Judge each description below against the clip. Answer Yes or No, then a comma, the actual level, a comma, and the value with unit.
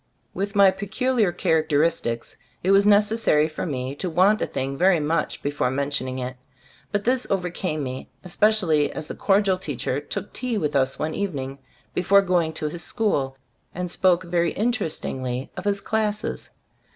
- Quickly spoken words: No, average, 165 wpm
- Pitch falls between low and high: Yes, medium, 175 Hz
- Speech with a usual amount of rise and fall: No, wide, 5.7 semitones